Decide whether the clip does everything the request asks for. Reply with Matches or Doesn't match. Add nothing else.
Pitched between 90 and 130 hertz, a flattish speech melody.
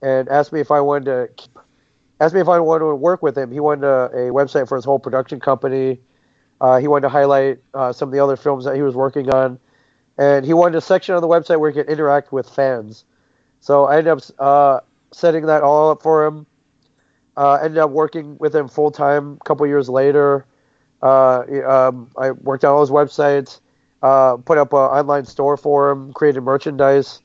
Doesn't match